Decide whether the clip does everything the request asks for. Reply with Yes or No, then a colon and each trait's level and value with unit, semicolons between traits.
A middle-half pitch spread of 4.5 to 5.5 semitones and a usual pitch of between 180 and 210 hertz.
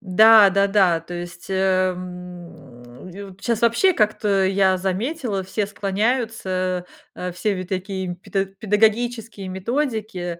No: average, 3.0 semitones; high, 190 Hz